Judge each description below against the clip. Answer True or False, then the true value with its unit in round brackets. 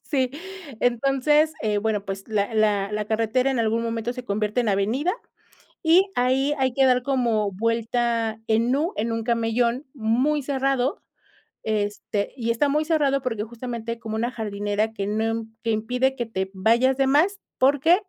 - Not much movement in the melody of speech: False (3.5 semitones)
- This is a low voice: False (235 Hz)